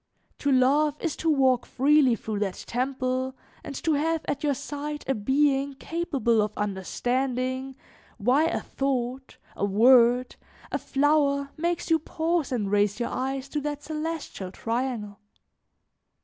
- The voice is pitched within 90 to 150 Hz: No, very high, 265 Hz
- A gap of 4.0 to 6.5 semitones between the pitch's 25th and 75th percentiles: No, average, 3.3 semitones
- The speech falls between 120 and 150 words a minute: Yes, average, 140 wpm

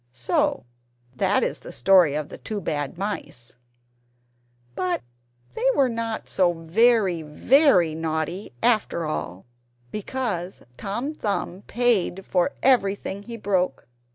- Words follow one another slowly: Yes, slow, 120 wpm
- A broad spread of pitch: Yes, wide, 5.8 semitones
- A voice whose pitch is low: No, high, 190 Hz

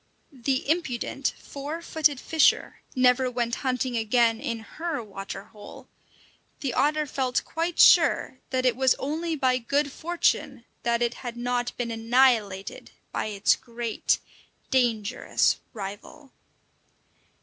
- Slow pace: Yes, slow, 125 wpm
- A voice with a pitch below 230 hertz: No, very high, 250 Hz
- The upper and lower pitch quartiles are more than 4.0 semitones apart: No, average, 3.2 semitones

